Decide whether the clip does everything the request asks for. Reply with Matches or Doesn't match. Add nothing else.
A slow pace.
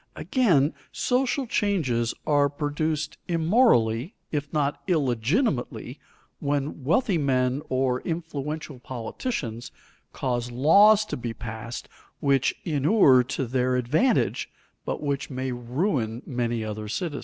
Matches